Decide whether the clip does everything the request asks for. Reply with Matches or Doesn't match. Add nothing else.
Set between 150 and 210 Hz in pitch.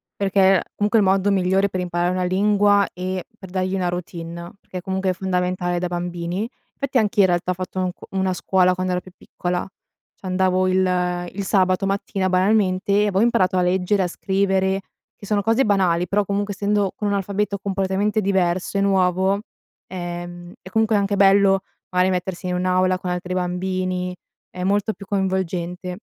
Matches